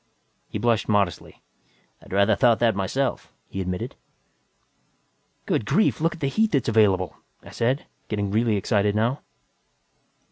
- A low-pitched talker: Yes, low, 110 Hz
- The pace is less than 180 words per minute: Yes, average, 140 wpm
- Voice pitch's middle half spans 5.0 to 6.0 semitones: No, average, 4.3 semitones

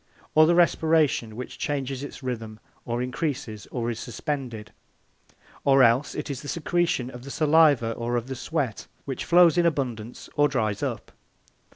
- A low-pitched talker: Yes, low, 130 Hz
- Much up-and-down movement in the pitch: No, average, 4.2 semitones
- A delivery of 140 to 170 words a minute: Yes, average, 165 wpm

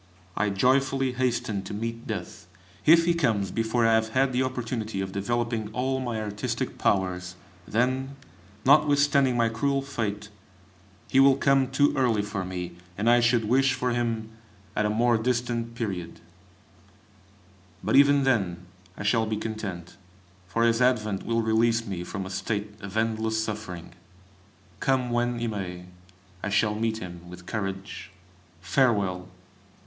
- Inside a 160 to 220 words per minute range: No, average, 150 wpm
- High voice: No, low, 115 Hz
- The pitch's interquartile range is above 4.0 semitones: No, average, 3.6 semitones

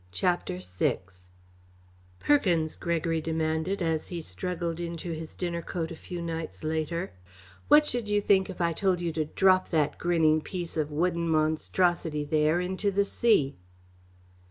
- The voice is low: No, medium, 170 Hz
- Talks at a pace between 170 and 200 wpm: No, average, 150 wpm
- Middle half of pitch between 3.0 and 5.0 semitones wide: No, narrow, 2.5 semitones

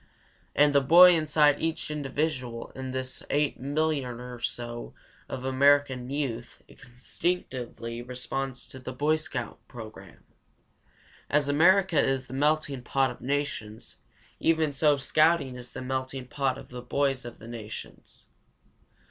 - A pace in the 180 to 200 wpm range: No, slow, 135 wpm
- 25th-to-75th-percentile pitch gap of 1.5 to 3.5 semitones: Yes, average, 3.0 semitones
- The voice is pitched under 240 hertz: Yes, low, 135 Hz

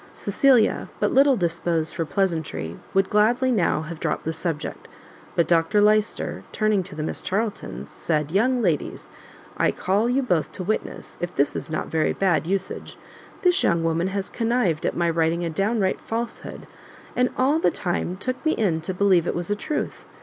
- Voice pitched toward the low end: No, high, 190 Hz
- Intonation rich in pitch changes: No, average, 5.0 semitones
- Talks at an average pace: Yes, average, 180 wpm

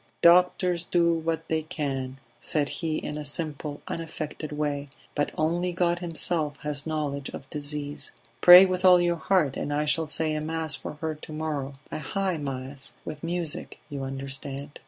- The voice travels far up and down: No, average, 2.8 semitones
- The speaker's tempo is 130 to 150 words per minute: No, average, 170 wpm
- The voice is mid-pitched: Yes, medium, 155 Hz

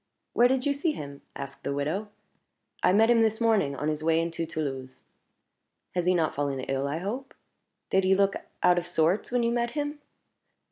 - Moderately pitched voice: Yes, medium, 180 Hz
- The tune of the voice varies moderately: No, wide, 7.7 semitones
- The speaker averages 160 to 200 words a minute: Yes, average, 195 wpm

